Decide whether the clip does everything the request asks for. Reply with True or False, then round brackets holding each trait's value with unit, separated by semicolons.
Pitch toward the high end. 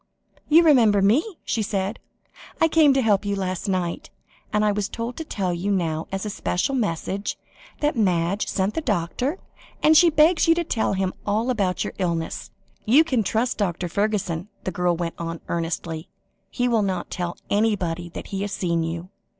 True (200 Hz)